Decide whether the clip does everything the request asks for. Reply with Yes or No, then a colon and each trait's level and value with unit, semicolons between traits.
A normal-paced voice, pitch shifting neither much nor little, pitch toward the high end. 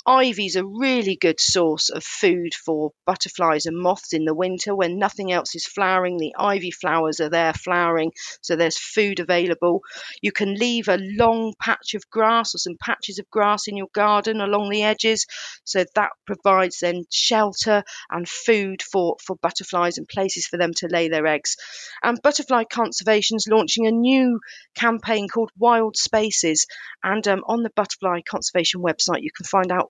Yes: average, 180 wpm; average, 4.1 semitones; high, 195 Hz